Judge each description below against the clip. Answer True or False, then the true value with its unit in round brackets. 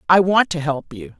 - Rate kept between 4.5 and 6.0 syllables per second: True (5.0 syllables/s)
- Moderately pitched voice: True (170 Hz)